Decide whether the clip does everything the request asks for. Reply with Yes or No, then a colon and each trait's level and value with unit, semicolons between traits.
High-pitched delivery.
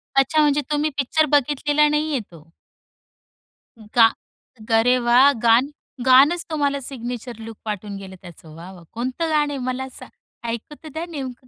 Yes: very high, 260 Hz